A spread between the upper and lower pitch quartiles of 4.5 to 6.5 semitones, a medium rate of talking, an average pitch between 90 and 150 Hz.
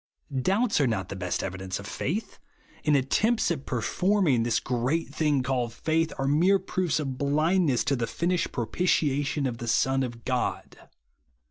Yes: wide, 5.5 semitones; average, 160 wpm; medium, 140 Hz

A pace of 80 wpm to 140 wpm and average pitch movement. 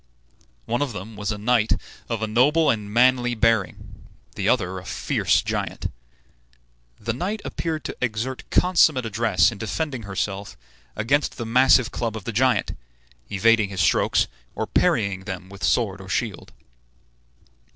No: average, 150 wpm; average, 3.9 semitones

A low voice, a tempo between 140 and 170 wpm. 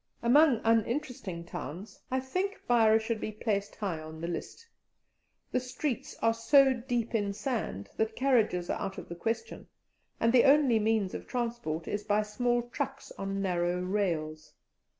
No: high, 220 Hz; average, 160 wpm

